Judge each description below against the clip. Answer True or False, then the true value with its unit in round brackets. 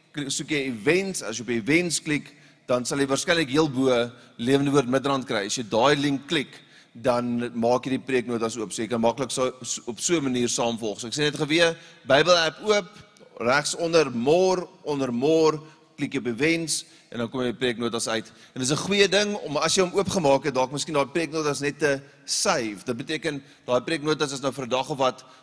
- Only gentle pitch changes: False (4.2 semitones)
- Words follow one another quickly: True (215 wpm)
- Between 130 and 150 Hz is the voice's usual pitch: True (140 Hz)